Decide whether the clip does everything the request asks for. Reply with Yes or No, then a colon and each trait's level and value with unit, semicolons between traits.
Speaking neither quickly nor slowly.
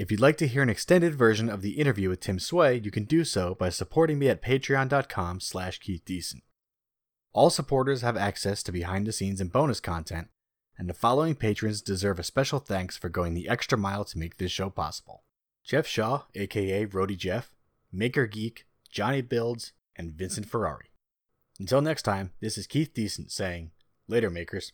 Yes: average, 180 wpm